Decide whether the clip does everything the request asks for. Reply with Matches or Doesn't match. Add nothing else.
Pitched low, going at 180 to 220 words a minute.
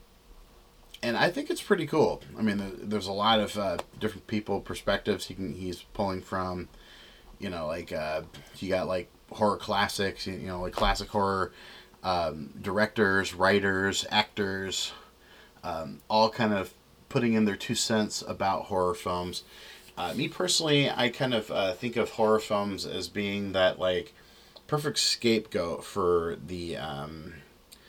Doesn't match